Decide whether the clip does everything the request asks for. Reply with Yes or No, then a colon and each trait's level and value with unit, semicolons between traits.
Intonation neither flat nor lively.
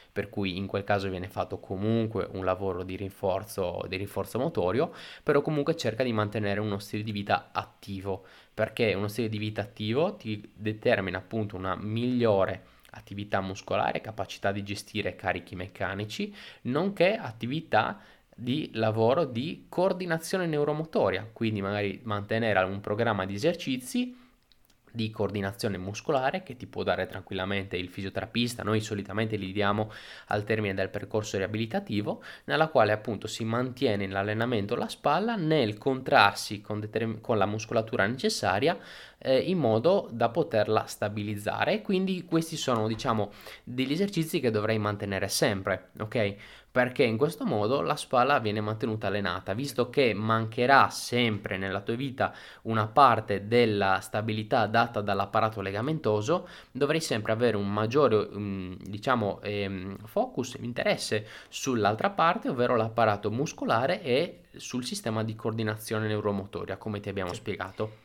Yes: average, 3.4 semitones